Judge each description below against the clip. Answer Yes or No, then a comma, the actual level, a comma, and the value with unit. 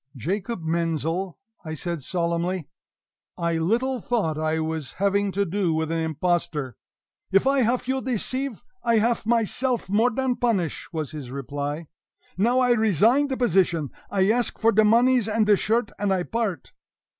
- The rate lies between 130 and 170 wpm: Yes, average, 160 wpm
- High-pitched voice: Yes, high, 195 Hz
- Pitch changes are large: Yes, wide, 6.2 semitones